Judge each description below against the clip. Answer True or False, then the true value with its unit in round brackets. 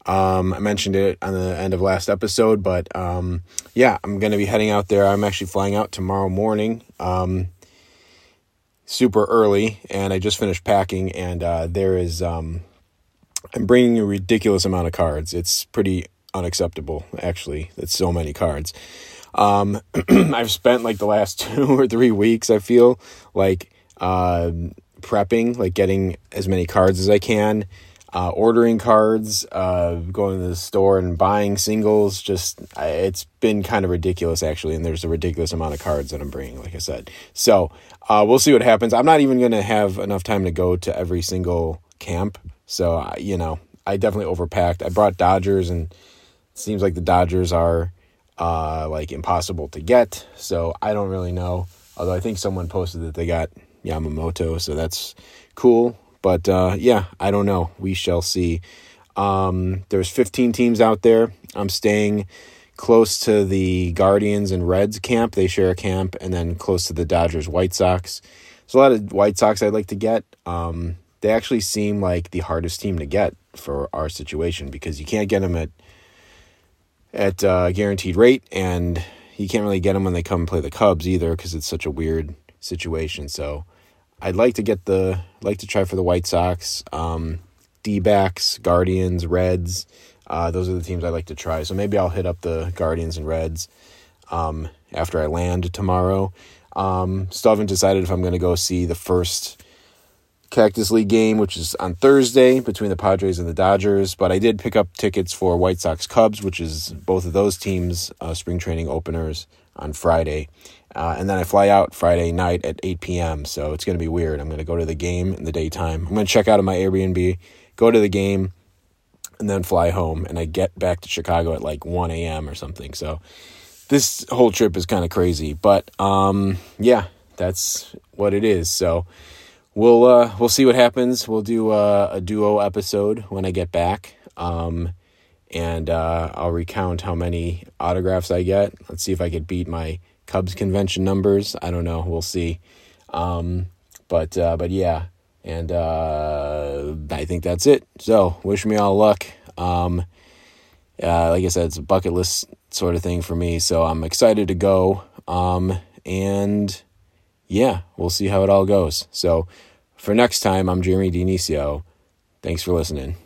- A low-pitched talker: True (90 Hz)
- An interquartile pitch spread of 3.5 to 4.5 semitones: False (2.8 semitones)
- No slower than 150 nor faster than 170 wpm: False (185 wpm)